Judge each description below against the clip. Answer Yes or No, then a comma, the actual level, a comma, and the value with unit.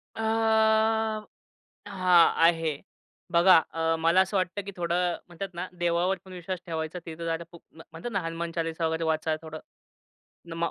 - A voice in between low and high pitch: Yes, medium, 170 Hz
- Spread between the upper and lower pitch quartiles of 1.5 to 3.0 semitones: Yes, average, 2.7 semitones